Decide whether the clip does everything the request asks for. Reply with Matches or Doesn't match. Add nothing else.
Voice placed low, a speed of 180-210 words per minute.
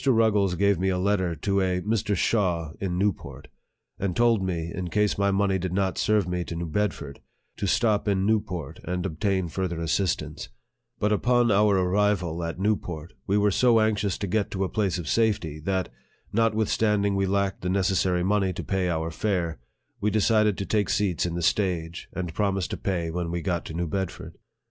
Matches